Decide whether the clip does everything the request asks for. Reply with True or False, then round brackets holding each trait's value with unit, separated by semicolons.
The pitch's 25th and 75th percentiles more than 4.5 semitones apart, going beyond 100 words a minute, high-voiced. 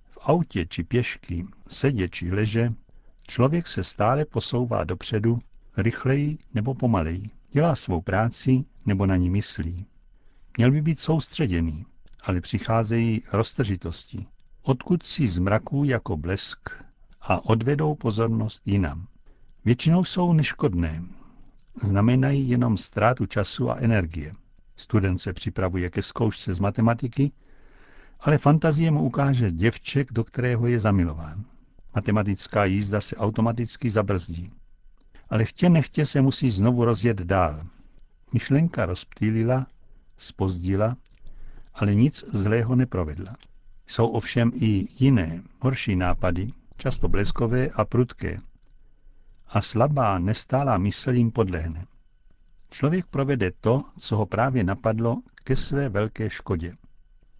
False (5.1 semitones; 115 wpm; 115 Hz)